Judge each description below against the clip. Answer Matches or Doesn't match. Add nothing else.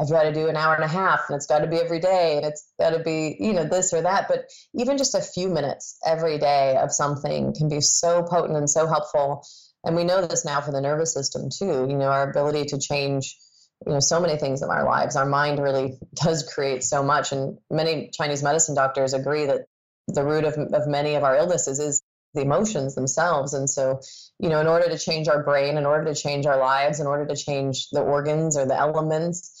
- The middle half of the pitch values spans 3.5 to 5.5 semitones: Doesn't match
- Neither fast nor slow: Doesn't match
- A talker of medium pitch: Matches